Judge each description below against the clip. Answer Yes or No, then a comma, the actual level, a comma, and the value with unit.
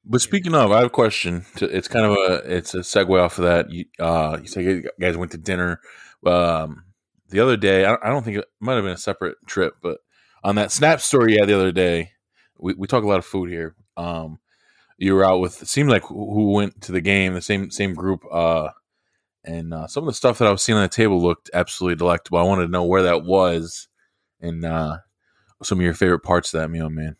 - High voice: No, very low, 90 Hz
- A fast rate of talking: Yes, fast, 245 wpm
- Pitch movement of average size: Yes, average, 3.0 semitones